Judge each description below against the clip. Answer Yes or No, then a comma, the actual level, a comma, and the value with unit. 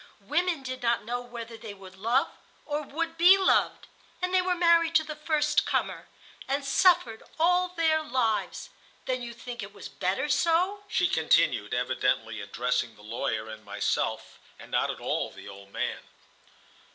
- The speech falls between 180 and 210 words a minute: No, average, 165 wpm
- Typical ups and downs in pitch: No, wide, 7.1 semitones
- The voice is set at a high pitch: Yes, very high, 275 Hz